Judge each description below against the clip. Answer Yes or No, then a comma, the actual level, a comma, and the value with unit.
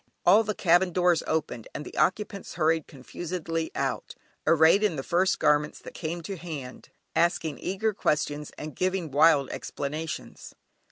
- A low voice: No, medium, 165 Hz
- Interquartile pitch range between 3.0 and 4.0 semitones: Yes, average, 3.4 semitones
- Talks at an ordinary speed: Yes, average, 150 wpm